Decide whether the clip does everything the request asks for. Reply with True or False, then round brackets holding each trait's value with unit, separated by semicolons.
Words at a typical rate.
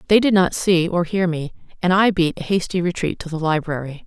False (235 wpm)